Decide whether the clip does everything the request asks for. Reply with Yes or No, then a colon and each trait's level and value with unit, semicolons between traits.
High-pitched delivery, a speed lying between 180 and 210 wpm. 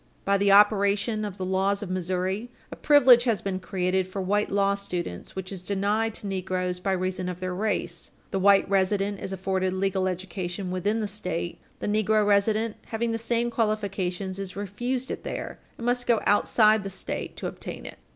Yes: high, 195 Hz; average, 190 wpm